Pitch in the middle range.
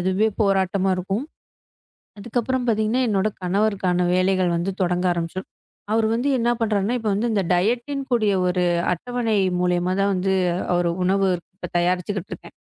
No: high, 195 Hz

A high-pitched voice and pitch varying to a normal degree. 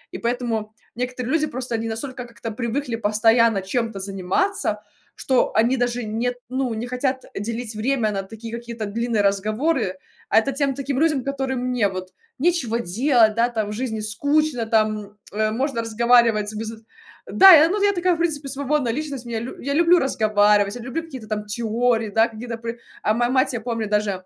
Yes: high, 235 Hz; average, 3.4 semitones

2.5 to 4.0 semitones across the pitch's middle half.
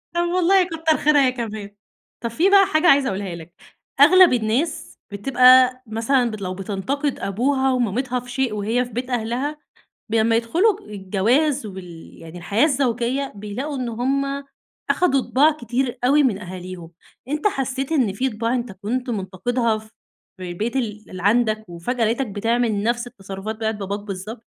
No: average, 4.6 semitones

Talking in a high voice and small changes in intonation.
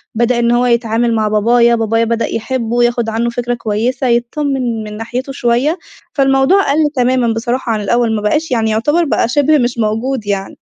Yes: high, 235 Hz; narrow, 2.3 semitones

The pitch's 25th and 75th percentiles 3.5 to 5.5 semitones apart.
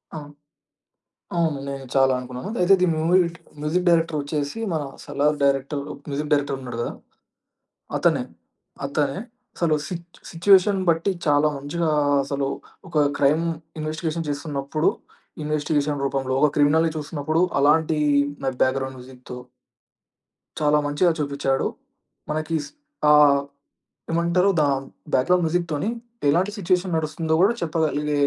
No: average, 2.8 semitones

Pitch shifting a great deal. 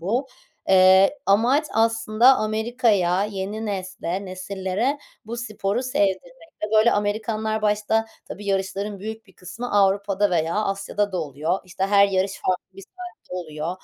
No: average, 2.7 semitones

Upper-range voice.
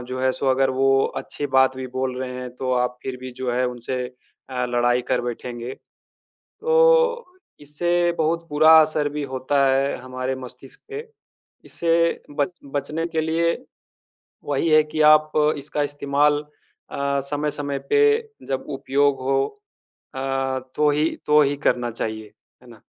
No: medium, 140 Hz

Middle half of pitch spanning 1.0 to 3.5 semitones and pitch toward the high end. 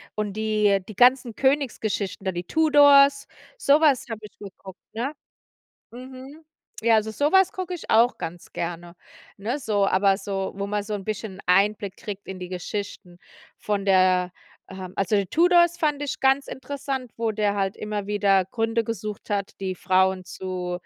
No: average, 5.3 semitones; high, 210 Hz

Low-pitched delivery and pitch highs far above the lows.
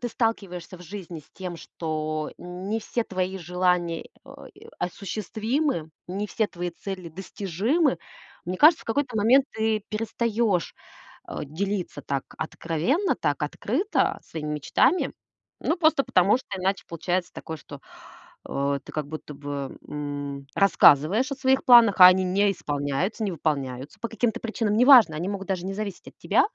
No: medium, 185 Hz; wide, 5.8 semitones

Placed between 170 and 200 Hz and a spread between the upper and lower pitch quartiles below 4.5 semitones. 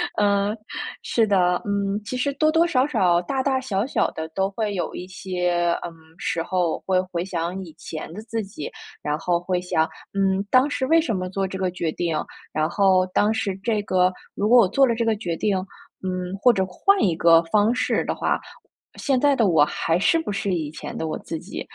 Yes: high, 190 Hz; average, 4.0 semitones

